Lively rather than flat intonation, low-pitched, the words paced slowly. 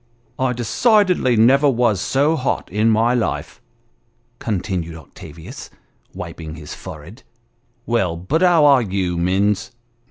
Yes: wide, 6.5 semitones; low, 110 Hz; slow, 125 wpm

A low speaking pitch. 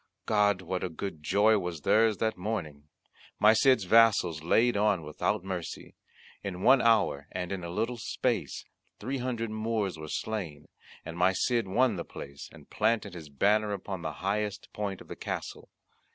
Yes: low, 100 Hz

